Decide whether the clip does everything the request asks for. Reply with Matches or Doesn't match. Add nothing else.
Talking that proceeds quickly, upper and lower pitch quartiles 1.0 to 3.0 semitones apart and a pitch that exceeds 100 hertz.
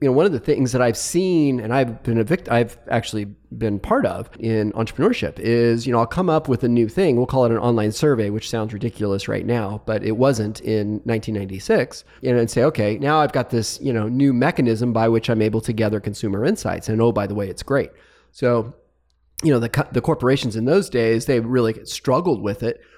Matches